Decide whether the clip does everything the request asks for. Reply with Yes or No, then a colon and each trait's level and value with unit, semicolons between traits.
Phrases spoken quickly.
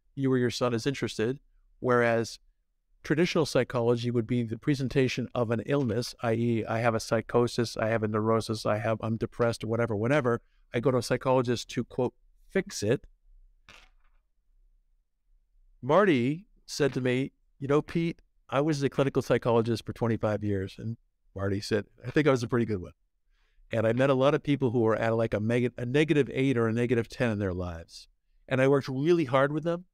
No: average, 190 wpm